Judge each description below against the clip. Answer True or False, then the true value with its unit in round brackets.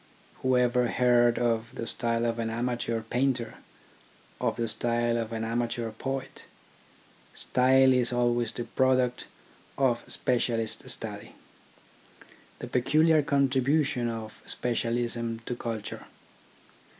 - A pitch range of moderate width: False (1.7 semitones)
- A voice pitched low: True (120 Hz)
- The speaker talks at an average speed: False (110 wpm)